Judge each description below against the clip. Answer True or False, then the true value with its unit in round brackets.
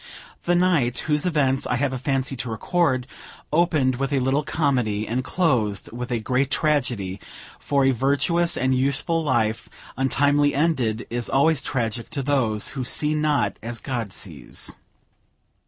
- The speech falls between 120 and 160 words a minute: True (155 wpm)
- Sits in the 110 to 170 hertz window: True (135 Hz)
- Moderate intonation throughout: True (3.6 semitones)